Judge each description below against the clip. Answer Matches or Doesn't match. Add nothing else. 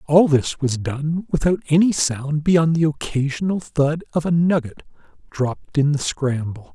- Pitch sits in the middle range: Matches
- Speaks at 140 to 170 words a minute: Matches